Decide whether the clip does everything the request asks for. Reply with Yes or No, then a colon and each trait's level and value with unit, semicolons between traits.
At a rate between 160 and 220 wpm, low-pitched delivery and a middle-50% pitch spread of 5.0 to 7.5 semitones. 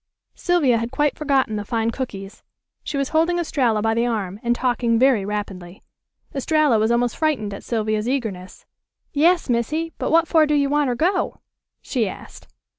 No: average, 170 wpm; high, 245 Hz; wide, 5.4 semitones